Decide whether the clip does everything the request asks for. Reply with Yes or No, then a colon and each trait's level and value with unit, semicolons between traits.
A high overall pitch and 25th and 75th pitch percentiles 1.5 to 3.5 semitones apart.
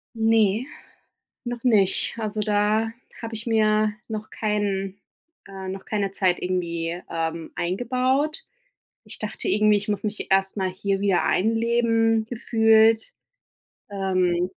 Yes: high, 210 Hz; average, 2.7 semitones